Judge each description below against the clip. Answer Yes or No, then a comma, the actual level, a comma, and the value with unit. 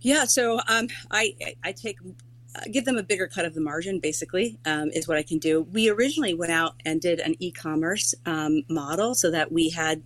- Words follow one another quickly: Yes, fast, 215 wpm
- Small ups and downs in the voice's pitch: No, average, 4.9 semitones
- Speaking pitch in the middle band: Yes, medium, 165 Hz